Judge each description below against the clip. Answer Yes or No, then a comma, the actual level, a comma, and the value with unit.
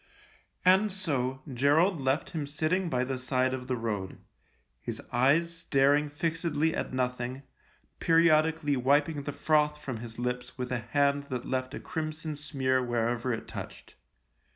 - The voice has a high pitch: No, medium, 140 Hz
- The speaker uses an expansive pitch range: No, average, 3.6 semitones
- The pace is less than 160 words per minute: Yes, average, 150 wpm